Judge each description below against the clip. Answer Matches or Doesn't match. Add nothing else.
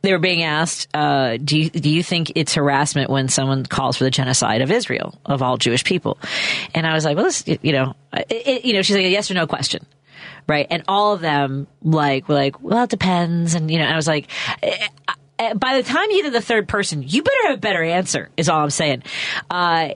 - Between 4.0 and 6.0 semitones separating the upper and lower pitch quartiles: Matches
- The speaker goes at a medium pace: Doesn't match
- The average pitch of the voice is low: Doesn't match